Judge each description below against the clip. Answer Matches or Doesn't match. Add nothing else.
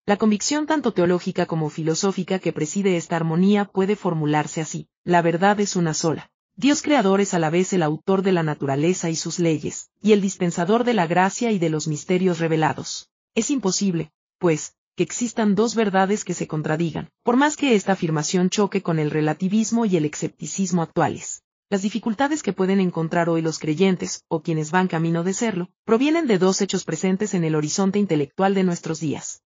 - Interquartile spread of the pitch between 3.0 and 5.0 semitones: Matches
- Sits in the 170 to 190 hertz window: Matches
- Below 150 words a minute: Doesn't match